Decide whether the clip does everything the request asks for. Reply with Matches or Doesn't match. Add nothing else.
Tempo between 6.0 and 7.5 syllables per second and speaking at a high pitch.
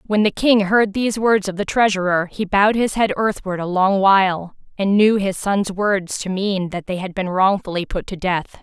Doesn't match